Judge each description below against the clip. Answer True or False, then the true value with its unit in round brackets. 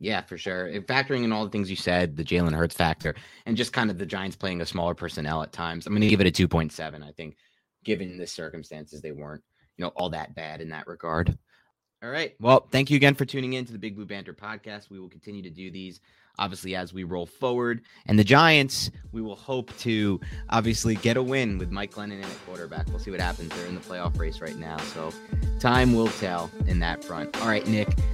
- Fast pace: True (245 wpm)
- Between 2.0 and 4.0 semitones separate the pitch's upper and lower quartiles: False (4.6 semitones)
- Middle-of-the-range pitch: False (95 Hz)